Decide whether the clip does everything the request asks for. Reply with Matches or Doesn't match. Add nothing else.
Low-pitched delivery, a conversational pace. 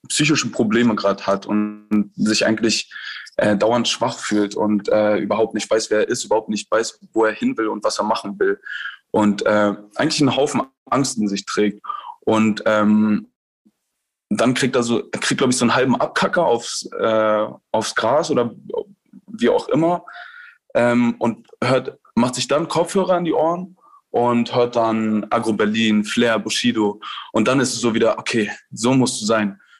Matches